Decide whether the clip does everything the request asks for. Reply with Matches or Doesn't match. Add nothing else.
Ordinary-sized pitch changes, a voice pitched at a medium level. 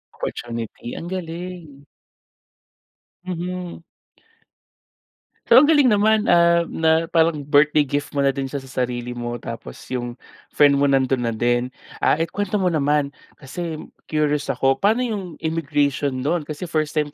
Matches